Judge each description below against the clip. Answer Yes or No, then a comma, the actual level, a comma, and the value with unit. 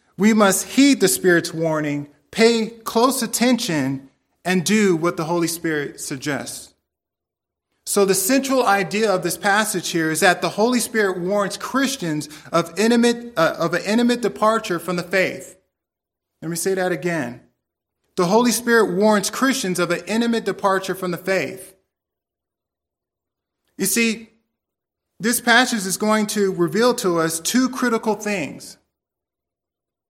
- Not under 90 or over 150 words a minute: Yes, average, 140 wpm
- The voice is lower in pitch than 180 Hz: No, high, 190 Hz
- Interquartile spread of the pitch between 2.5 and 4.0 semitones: No, average, 5.3 semitones